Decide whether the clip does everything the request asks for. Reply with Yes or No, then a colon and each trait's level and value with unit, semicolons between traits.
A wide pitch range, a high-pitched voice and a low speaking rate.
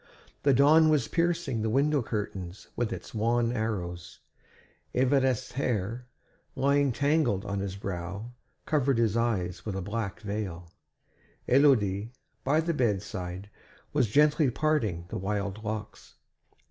No: wide, 5.7 semitones; low, 115 Hz; slow, 125 wpm